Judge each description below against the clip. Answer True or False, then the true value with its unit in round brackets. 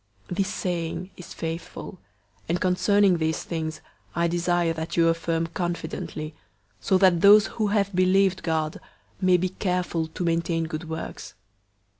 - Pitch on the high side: False (175 Hz)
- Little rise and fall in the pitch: True (2.1 semitones)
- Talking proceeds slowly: False (145 wpm)